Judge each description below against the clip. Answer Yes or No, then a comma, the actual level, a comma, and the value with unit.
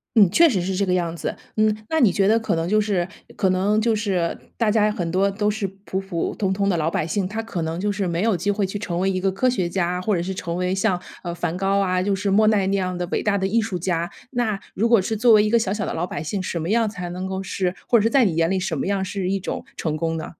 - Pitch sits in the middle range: No, high, 195 Hz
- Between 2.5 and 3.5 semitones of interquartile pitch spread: Yes, average, 2.9 semitones